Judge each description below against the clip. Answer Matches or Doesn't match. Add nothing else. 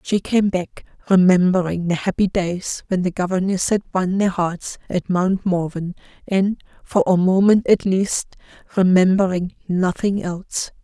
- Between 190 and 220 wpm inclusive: Doesn't match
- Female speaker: Matches